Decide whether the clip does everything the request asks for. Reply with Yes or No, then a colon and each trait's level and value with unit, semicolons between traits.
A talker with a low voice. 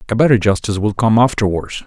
Yes: low, 110 Hz